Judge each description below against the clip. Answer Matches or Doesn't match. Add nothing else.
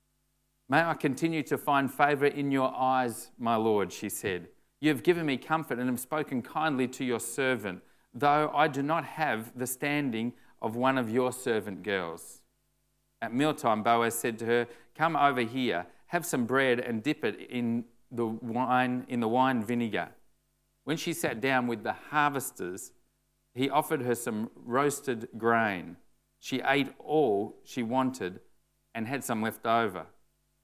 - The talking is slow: Doesn't match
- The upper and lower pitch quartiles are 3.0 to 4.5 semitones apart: Matches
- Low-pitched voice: Matches